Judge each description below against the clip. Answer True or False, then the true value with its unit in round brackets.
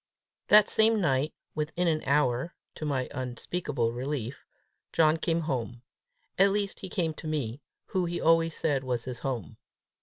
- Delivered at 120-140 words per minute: False (155 wpm)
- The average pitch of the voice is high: False (150 Hz)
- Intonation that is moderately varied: True (4.6 semitones)